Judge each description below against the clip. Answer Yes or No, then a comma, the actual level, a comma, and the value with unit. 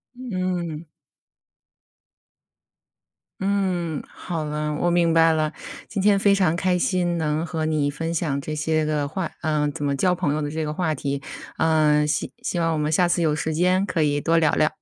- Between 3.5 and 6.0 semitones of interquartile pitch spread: No, average, 2.7 semitones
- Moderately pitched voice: Yes, medium, 160 Hz